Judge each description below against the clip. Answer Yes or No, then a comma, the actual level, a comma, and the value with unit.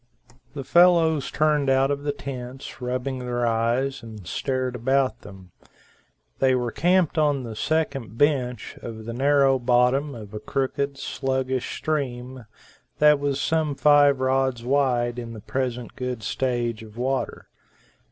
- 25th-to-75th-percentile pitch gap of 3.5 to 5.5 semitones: No, narrow, 2.6 semitones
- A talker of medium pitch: No, low, 130 Hz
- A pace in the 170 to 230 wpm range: No, average, 140 wpm